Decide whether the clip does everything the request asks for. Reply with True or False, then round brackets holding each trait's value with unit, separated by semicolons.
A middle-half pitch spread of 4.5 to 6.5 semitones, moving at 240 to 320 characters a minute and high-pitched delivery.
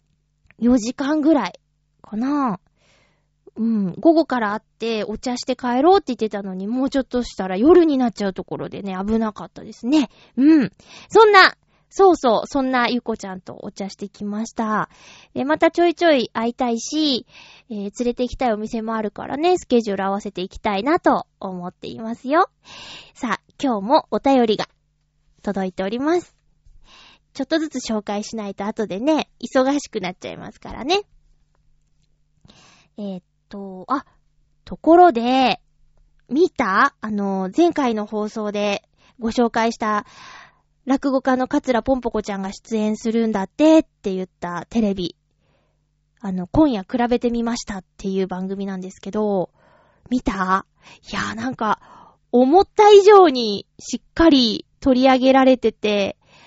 True (5.3 semitones; 305 characters per minute; 225 Hz)